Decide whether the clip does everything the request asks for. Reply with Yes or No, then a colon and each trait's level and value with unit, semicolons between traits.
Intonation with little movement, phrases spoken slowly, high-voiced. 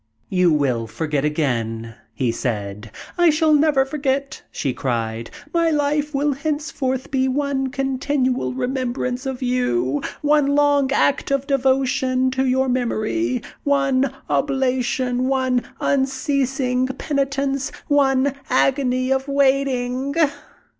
Yes: narrow, 2.1 semitones; slow, 115 wpm; very high, 265 Hz